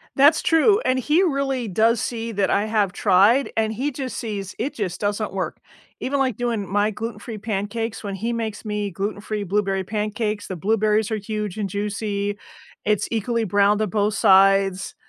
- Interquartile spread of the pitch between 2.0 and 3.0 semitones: Yes, narrow, 2.4 semitones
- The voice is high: Yes, high, 210 Hz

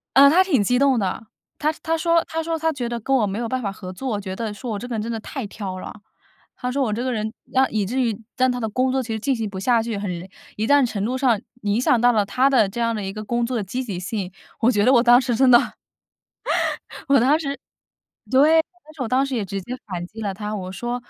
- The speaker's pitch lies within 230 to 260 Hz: Yes, high, 235 Hz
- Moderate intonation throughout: Yes, average, 4.0 semitones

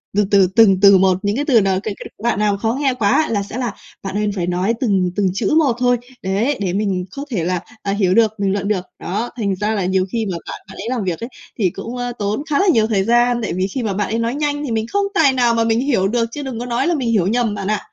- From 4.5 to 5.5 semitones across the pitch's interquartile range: No, average, 3.8 semitones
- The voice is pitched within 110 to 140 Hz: No, high, 215 Hz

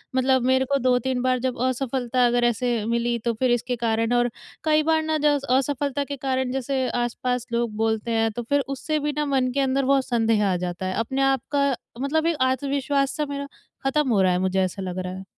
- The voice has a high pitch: Yes, very high, 255 Hz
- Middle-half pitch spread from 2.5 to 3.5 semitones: Yes, average, 2.8 semitones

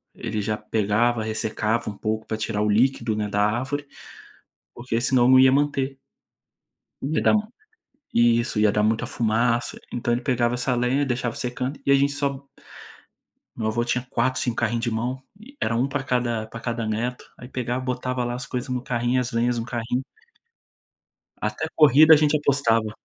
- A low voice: Yes, low, 120 Hz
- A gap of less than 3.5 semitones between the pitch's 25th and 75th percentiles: Yes, narrow, 2.5 semitones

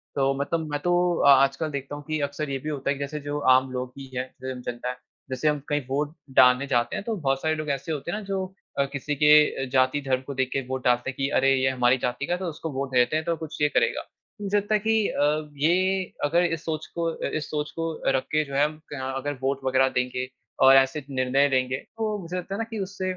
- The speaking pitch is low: No, medium, 145 Hz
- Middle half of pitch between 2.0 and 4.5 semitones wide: Yes, average, 3.2 semitones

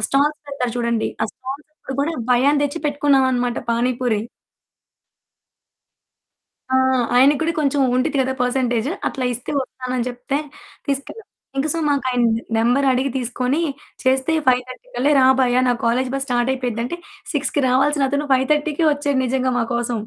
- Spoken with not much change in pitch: Yes, narrow, 2.3 semitones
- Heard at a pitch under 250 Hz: No, very high, 260 Hz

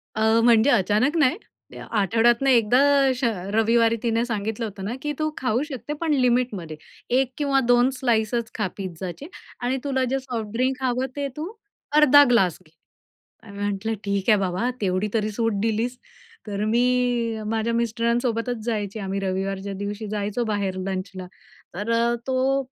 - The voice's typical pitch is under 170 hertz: No, high, 230 Hz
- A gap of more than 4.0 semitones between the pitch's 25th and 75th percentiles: No, average, 3.5 semitones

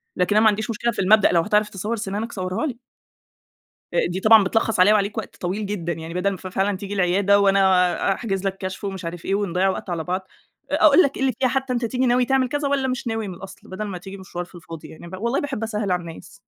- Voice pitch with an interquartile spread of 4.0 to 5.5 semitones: No, average, 3.3 semitones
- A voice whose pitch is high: Yes, high, 200 Hz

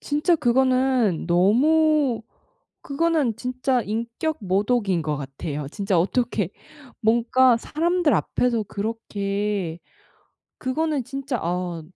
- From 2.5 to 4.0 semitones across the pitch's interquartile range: No, wide, 5.5 semitones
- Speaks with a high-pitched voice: Yes, high, 235 Hz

